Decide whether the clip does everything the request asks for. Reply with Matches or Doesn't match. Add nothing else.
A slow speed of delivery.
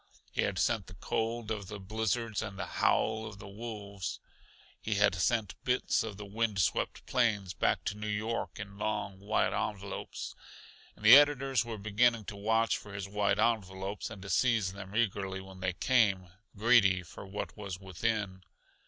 Doesn't match